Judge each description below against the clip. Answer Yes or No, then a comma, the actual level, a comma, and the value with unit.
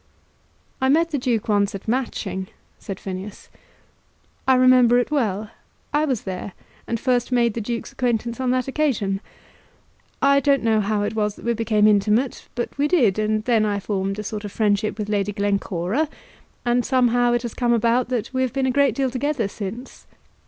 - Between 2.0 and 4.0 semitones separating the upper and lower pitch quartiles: Yes, average, 3.7 semitones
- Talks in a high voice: Yes, high, 230 Hz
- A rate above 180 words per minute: Yes, average, 190 wpm